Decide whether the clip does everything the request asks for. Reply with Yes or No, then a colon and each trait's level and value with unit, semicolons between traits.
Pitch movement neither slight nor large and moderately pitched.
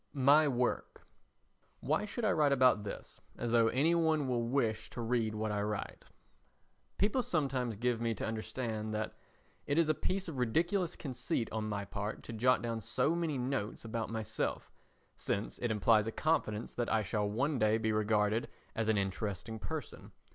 No: average, 4.6 semitones; low, 115 Hz